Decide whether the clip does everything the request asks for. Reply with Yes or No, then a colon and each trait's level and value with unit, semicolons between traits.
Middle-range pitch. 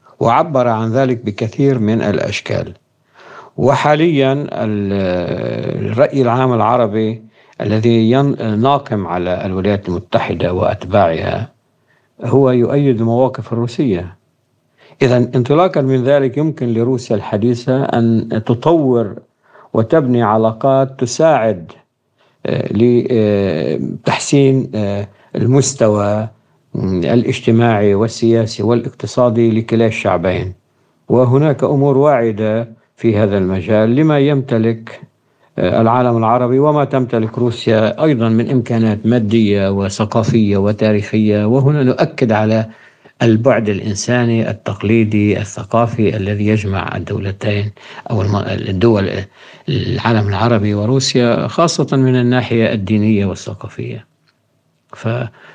No: low, 115 Hz